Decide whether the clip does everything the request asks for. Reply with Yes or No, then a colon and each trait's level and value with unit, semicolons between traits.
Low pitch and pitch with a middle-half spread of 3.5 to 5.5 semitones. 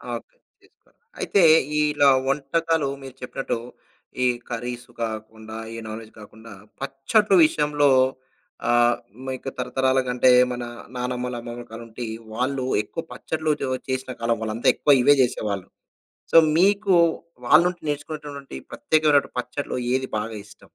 Yes: low, 130 Hz; average, 3.8 semitones